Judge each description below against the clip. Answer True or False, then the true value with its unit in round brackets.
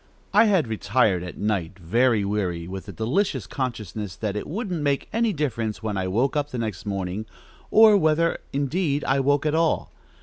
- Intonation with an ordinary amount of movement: False (7.0 semitones)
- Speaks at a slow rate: False (180 wpm)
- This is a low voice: True (120 Hz)